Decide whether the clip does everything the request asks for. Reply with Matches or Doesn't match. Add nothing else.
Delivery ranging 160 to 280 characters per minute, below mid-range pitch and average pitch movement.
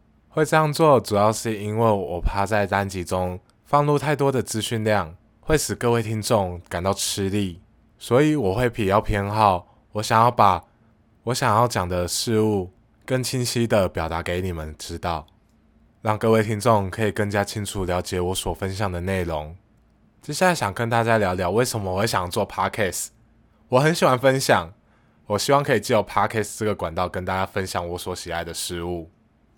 Doesn't match